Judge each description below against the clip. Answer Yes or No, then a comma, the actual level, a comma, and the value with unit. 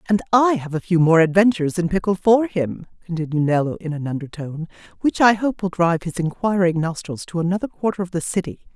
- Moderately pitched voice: Yes, medium, 180 Hz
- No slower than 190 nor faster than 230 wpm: Yes, fast, 205 wpm